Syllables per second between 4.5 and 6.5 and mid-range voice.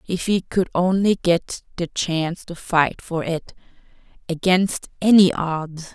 No: 3.9 syllables/s; medium, 175 Hz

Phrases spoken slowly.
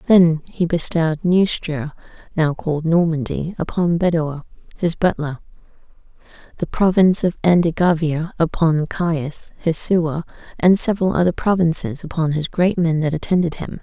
Yes: slow, 130 wpm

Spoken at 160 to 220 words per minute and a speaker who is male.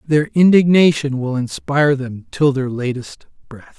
No: average, 145 wpm; male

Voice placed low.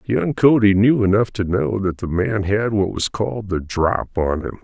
Yes: low, 100 Hz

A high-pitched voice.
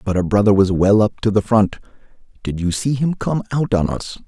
No: low, 105 Hz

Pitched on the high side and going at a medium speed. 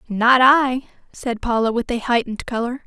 Yes: high, 240 Hz; average, 170 wpm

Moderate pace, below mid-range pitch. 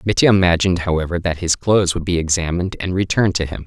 No: fast, 215 wpm; very low, 90 Hz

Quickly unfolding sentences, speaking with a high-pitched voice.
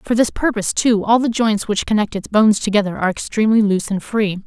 Yes: fast, 230 wpm; high, 210 Hz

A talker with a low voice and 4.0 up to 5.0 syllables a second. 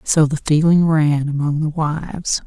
No: medium, 155 Hz; 4.3 syllables/s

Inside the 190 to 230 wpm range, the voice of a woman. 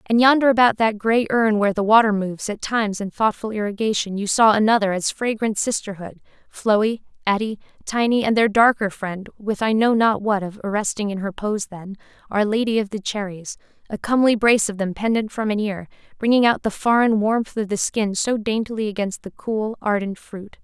Yes: average, 200 wpm; female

